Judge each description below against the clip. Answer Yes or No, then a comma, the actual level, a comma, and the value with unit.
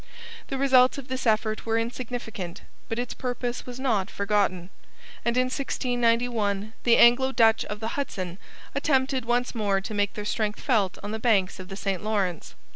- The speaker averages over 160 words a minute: Yes, average, 175 wpm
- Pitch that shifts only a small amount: No, average, 3.6 semitones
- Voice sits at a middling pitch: No, high, 225 Hz